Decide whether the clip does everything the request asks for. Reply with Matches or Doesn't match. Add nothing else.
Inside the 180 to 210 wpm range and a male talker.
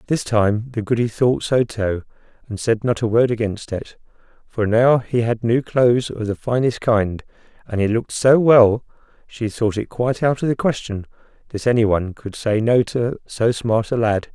Matches